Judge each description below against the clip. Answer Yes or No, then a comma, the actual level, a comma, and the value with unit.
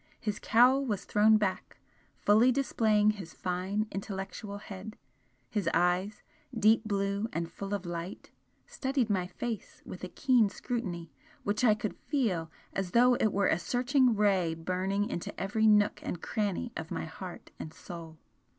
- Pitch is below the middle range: No, high, 205 Hz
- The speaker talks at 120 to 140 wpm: No, average, 155 wpm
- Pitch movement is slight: No, average, 3.3 semitones